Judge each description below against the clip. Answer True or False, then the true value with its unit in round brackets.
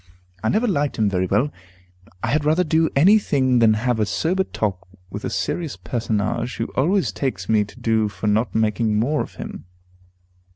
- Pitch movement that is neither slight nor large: False (6.1 semitones)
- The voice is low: True (120 Hz)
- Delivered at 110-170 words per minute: False (190 wpm)